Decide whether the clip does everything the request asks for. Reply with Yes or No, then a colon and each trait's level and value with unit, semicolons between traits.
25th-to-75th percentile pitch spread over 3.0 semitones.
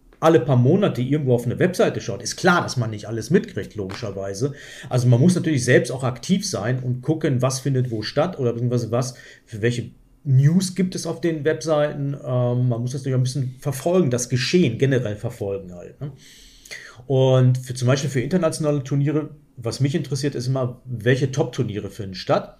Yes: average, 3.6 semitones